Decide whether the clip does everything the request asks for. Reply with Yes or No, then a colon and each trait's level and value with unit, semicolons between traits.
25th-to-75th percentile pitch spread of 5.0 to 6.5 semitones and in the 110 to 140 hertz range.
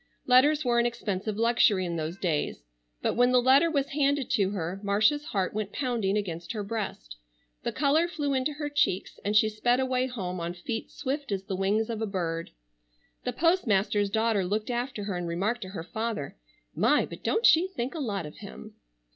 No: average, 5.3 semitones; high, 220 Hz